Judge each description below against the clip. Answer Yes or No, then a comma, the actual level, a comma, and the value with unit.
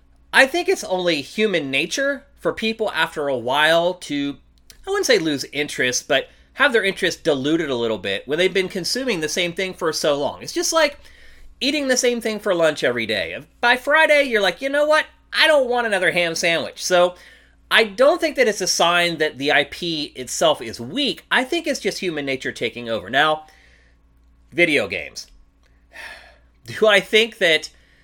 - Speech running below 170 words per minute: No, average, 190 wpm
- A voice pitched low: No, medium, 185 Hz